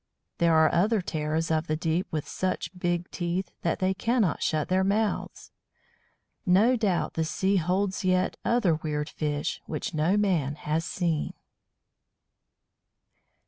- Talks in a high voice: No, medium, 175 Hz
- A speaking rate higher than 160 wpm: No, average, 140 wpm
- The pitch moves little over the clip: No, average, 3.2 semitones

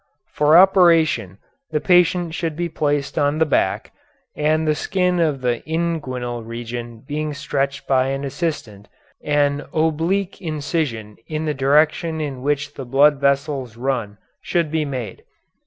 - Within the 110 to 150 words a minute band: Yes, average, 140 wpm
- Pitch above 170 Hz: No, medium, 145 Hz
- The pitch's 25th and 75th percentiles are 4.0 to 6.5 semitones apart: No, average, 3.3 semitones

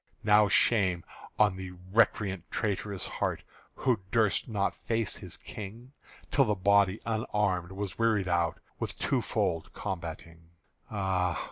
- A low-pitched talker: Yes, low, 100 Hz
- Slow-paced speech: Yes, slow, 130 wpm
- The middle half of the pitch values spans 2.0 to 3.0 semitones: Yes, average, 2.7 semitones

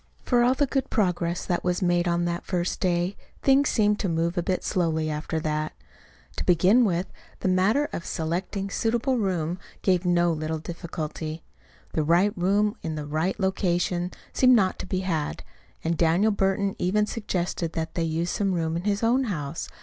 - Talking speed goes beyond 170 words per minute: Yes, average, 185 wpm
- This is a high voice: No, medium, 180 Hz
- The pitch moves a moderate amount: Yes, average, 3.3 semitones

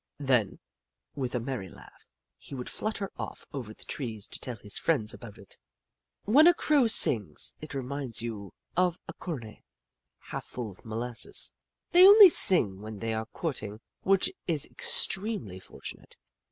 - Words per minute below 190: Yes, average, 155 wpm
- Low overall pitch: Yes, low, 125 Hz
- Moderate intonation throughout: No, wide, 8.5 semitones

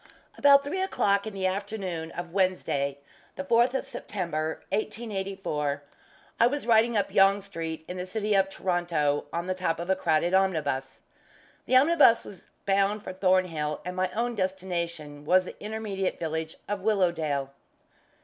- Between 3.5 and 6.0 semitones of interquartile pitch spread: Yes, average, 4.0 semitones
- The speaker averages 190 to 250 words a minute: No, average, 155 wpm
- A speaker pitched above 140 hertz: Yes, medium, 185 Hz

